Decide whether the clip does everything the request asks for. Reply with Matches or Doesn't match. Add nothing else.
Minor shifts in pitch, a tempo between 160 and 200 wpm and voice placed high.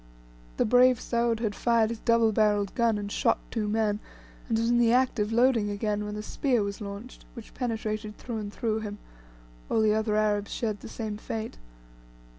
Matches